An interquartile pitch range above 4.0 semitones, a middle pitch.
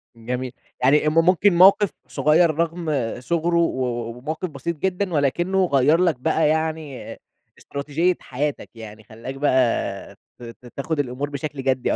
Yes: average, 4.6 semitones; medium, 150 Hz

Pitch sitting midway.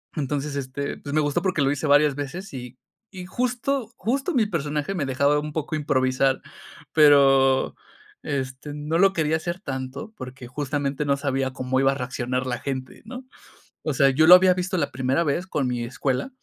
Yes: medium, 145 Hz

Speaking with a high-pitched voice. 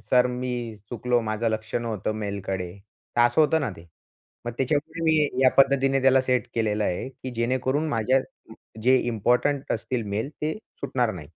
No: low, 125 Hz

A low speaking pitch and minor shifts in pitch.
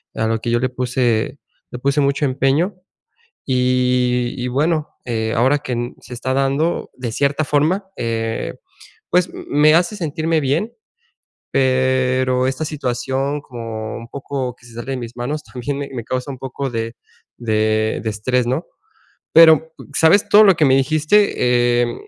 No: low, 130 Hz; average, 3.3 semitones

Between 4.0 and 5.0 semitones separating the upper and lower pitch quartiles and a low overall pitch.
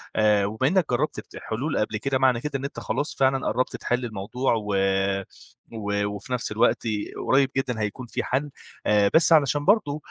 Yes: average, 4.5 semitones; low, 125 Hz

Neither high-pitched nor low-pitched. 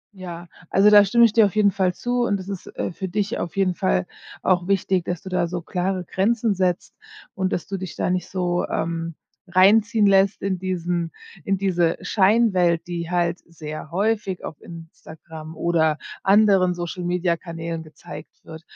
Yes: medium, 180 Hz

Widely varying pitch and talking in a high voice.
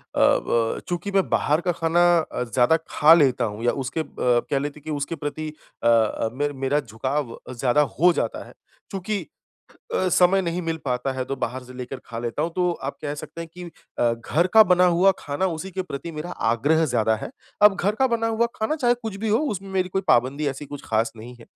No: wide, 6.2 semitones; medium, 150 Hz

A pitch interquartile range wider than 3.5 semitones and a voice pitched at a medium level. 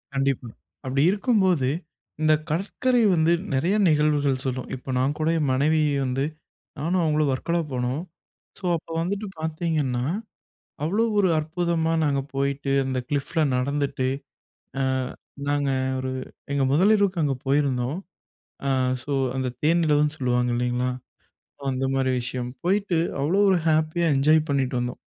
Yes: average, 3.9 semitones; medium, 145 Hz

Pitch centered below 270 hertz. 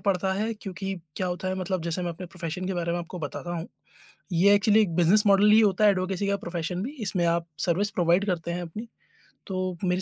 Yes: medium, 185 Hz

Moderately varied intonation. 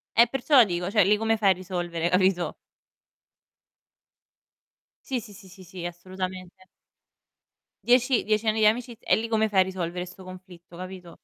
Yes: average, 3.4 semitones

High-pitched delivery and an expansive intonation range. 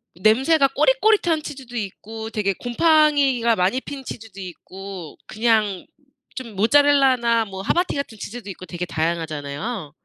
Yes: high, 225 Hz; wide, 6.1 semitones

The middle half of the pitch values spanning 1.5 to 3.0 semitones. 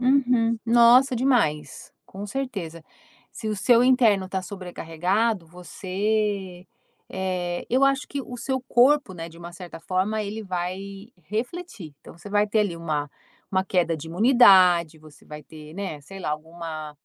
No: average, 5.3 semitones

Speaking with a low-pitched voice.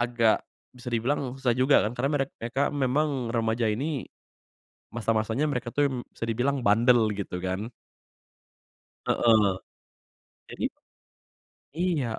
Yes: low, 120 Hz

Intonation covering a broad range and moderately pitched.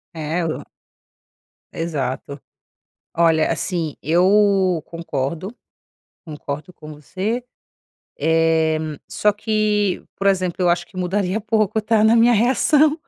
No: average, 4.6 semitones; medium, 180 Hz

